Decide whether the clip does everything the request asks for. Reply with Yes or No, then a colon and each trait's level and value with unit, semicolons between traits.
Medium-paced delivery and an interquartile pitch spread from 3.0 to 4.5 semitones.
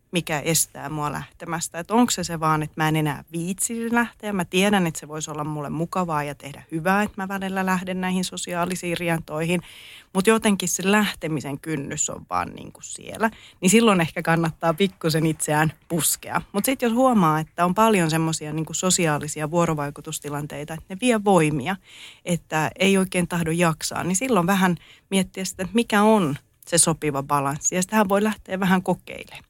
No: fast, 170 wpm; average, 3.6 semitones